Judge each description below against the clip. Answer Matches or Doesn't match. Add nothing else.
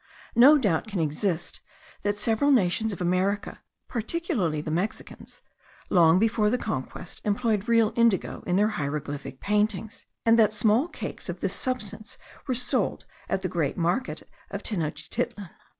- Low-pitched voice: Doesn't match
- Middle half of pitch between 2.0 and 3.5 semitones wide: Doesn't match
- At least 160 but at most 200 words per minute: Doesn't match